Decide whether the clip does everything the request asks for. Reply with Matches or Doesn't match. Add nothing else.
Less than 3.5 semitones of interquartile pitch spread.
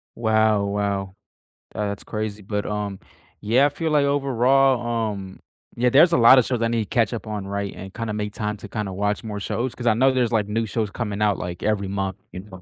Matches